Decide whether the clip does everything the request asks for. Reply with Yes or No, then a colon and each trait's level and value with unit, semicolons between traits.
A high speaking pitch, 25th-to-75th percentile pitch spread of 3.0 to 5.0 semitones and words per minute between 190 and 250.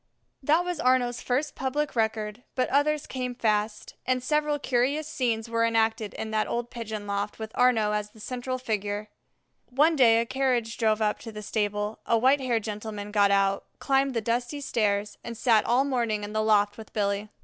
Yes: high, 230 Hz; average, 3.3 semitones; average, 195 wpm